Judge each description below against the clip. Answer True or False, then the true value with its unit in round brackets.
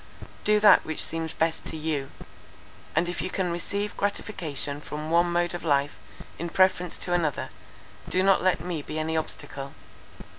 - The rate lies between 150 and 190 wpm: True (170 wpm)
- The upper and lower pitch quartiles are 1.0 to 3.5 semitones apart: True (2.8 semitones)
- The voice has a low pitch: False (170 Hz)